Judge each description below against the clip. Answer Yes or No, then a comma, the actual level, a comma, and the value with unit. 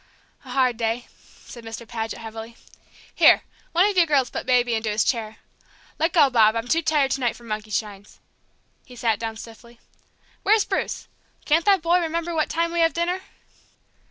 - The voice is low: No, high, 245 Hz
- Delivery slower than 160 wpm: No, average, 185 wpm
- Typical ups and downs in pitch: No, wide, 6.6 semitones